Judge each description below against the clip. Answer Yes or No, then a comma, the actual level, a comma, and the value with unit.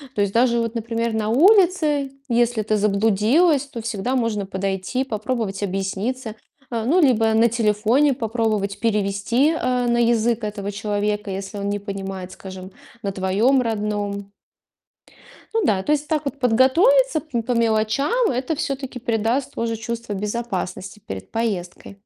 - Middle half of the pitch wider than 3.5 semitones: Yes, average, 3.9 semitones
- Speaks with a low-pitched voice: No, high, 225 Hz